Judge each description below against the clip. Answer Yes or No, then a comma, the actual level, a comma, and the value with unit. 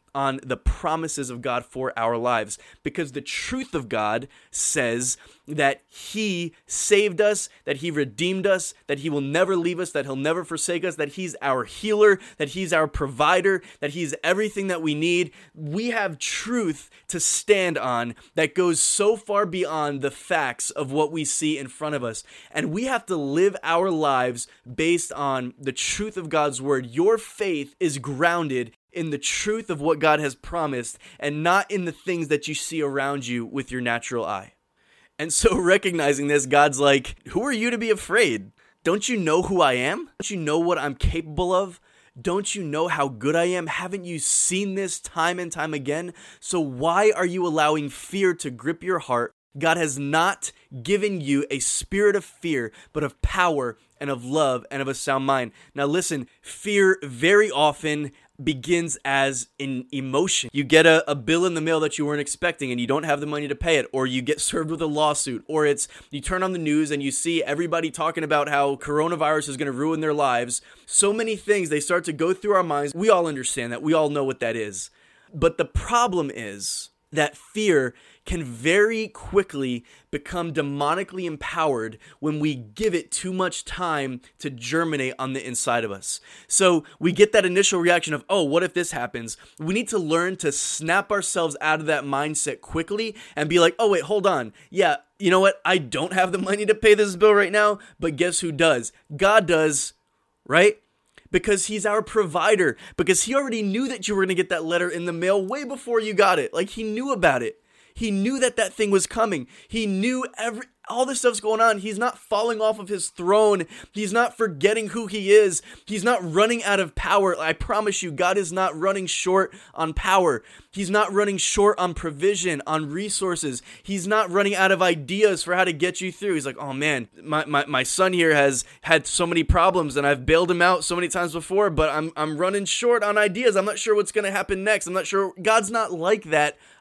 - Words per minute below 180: No, fast, 205 wpm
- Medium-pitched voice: Yes, medium, 170 Hz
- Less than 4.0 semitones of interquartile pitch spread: No, average, 5.3 semitones